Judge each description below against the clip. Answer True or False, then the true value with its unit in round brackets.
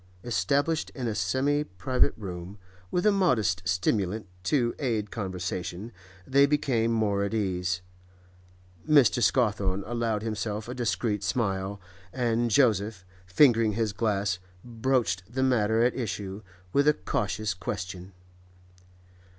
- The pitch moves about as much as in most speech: True (4.2 semitones)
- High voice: False (110 Hz)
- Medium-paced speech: False (120 wpm)